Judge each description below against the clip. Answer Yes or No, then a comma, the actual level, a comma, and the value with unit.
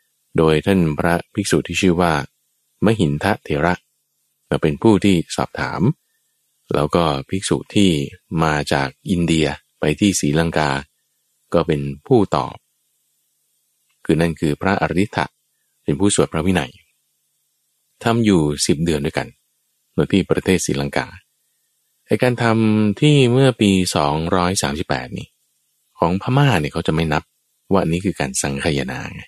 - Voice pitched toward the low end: Yes, very low, 80 Hz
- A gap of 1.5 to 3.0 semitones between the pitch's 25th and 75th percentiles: No, average, 4.7 semitones